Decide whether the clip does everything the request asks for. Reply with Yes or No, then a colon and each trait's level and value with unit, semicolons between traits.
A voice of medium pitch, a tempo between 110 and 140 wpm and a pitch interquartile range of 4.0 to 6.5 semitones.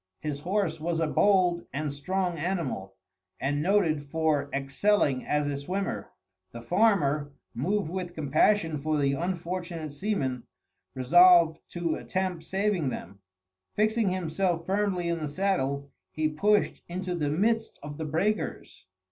Yes: medium, 165 Hz; slow, 135 wpm; average, 4.5 semitones